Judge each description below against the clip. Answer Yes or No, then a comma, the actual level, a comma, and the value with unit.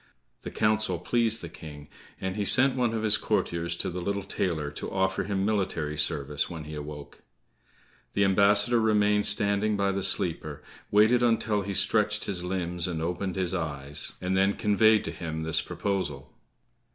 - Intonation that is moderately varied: Yes, average, 4.3 semitones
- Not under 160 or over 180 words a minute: Yes, average, 170 wpm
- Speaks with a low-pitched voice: Yes, very low, 95 Hz